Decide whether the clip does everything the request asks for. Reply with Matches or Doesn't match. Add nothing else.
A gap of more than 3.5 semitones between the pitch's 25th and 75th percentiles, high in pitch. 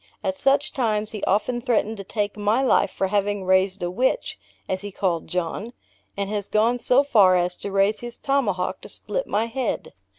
Matches